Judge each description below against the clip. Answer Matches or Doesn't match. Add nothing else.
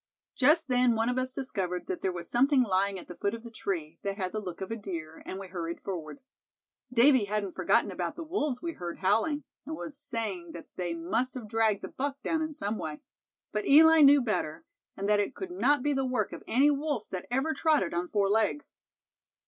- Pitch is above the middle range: Matches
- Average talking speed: Doesn't match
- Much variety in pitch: Matches